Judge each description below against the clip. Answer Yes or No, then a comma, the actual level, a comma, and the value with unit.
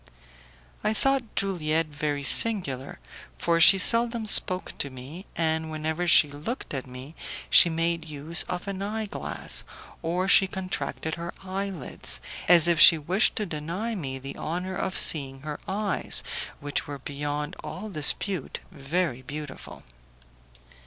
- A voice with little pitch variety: No, average, 4.5 semitones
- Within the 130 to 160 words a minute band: Yes, average, 145 wpm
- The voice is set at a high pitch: No, medium, 165 Hz